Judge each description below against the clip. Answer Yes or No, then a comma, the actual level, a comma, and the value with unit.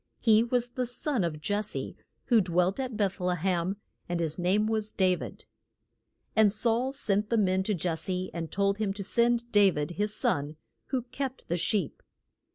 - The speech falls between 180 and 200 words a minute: Yes, average, 185 wpm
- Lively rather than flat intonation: No, average, 4.3 semitones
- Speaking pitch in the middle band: No, high, 205 Hz